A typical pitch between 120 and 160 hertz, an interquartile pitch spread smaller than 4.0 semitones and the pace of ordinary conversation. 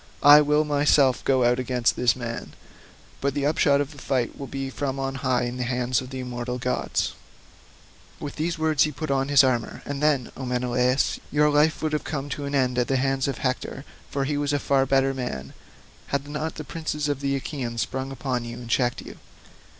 No: low, 135 Hz; narrow, 2.4 semitones; fast, 220 wpm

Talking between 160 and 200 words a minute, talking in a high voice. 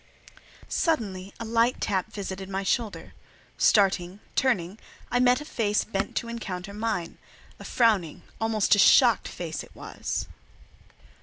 No: slow, 135 wpm; high, 210 Hz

